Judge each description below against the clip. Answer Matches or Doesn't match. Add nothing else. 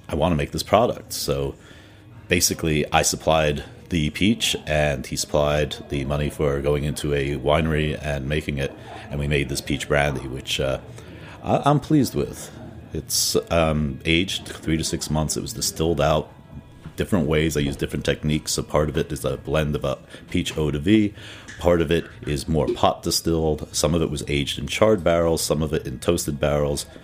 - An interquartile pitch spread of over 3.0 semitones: Doesn't match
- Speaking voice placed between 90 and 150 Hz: Doesn't match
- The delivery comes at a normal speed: Matches